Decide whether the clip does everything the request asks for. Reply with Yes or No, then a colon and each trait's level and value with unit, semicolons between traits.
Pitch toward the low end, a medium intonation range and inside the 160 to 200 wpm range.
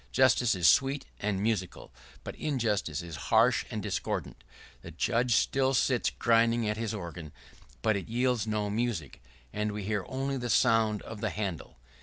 Yes: low, 110 Hz; average, 3.5 semitones; average, 165 wpm